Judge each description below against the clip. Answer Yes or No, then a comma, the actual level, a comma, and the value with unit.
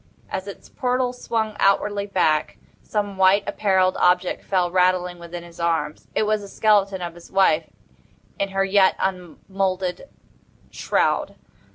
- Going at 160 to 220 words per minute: No, average, 140 wpm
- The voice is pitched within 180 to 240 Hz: Yes, high, 190 Hz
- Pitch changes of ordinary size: No, narrow, 2.2 semitones